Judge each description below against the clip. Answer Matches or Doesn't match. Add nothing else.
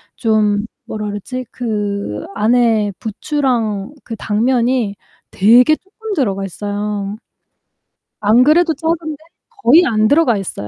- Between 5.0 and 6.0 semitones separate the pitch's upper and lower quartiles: Doesn't match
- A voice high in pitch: Matches